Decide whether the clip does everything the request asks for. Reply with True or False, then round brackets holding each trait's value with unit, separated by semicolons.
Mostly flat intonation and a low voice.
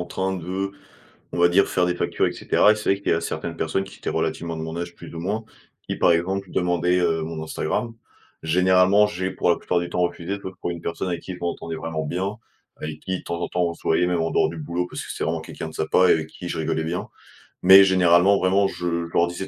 True (2.0 semitones; 90 Hz)